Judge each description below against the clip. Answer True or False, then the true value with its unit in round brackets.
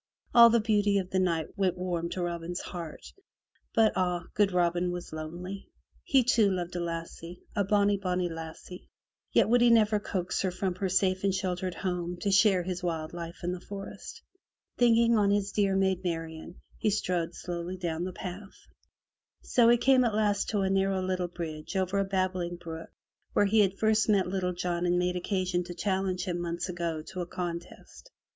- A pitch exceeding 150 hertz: True (185 Hz)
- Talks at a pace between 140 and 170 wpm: False (190 wpm)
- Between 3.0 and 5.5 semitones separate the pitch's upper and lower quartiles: False (2.4 semitones)